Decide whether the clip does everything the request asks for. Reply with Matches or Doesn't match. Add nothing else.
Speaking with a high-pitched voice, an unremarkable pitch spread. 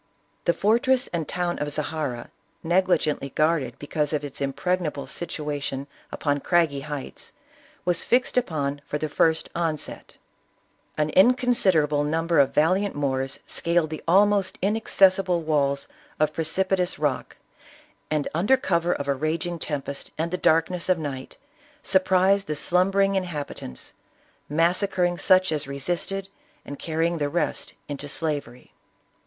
Doesn't match